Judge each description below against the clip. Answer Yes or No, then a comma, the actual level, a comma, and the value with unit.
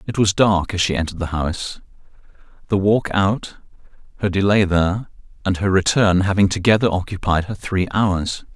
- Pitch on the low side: Yes, very low, 95 Hz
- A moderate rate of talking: Yes, average, 155 wpm